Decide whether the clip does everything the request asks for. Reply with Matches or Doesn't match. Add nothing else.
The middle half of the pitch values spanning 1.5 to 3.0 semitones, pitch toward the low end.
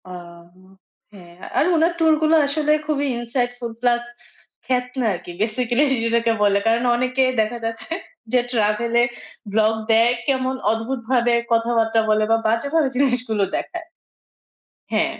Doesn't match